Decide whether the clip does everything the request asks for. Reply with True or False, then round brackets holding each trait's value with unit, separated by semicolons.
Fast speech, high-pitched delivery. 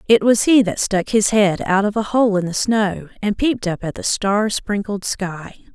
True (230 wpm; 205 Hz)